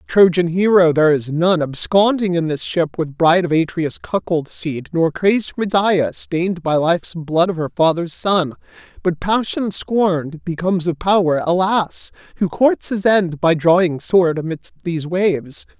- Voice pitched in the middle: Yes, medium, 175 Hz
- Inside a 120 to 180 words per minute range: Yes, average, 165 wpm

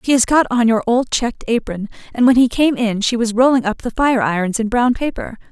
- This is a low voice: No, high, 235 Hz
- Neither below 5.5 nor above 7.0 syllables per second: Yes, 5.7 syllables/s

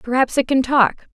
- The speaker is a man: No, female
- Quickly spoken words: Yes, fast, 210 wpm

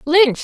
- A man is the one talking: No, female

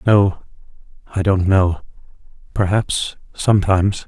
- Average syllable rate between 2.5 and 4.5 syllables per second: Yes, 4.3 syllables/s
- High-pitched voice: No, very low, 95 Hz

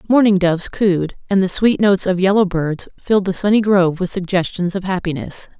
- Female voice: Yes, female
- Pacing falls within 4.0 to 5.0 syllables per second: No, 5.6 syllables/s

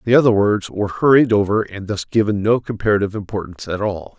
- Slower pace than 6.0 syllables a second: No, 6.5 syllables/s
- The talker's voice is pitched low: Yes, low, 105 Hz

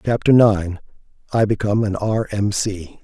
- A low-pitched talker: Yes, low, 105 Hz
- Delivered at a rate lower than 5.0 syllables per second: Yes, 4.6 syllables/s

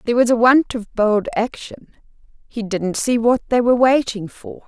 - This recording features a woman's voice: Yes, female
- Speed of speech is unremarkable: Yes, average, 195 wpm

